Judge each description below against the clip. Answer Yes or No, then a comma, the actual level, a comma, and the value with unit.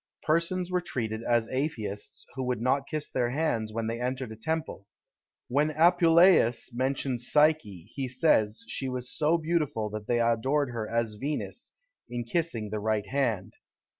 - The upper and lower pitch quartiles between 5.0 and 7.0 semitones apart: Yes, average, 5.3 semitones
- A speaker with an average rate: Yes, average, 160 wpm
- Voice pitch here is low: Yes, low, 125 Hz